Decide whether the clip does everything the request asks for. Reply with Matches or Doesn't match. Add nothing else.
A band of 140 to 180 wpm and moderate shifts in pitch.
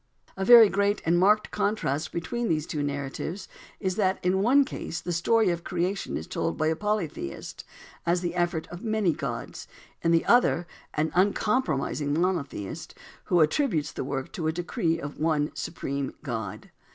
Matches